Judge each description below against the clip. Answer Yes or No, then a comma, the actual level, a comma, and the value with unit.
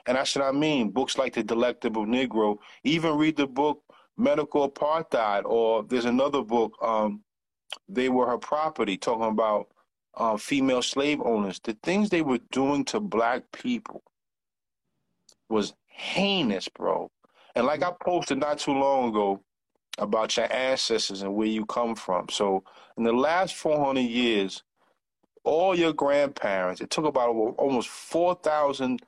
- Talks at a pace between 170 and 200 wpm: No, average, 150 wpm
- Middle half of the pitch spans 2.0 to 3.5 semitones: No, average, 5.3 semitones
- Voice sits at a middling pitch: No, low, 130 Hz